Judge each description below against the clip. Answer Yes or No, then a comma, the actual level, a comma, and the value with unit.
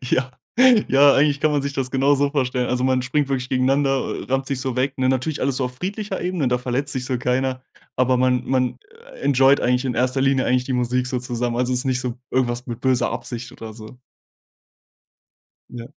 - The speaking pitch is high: No, low, 130 Hz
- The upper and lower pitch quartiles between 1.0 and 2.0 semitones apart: Yes, narrow, 1.5 semitones